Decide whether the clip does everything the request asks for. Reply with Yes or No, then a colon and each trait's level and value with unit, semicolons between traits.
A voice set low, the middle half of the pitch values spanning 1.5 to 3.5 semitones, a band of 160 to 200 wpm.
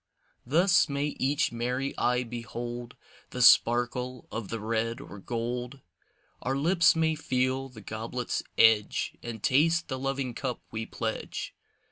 No: low, 125 Hz; average, 2.8 semitones; slow, 135 wpm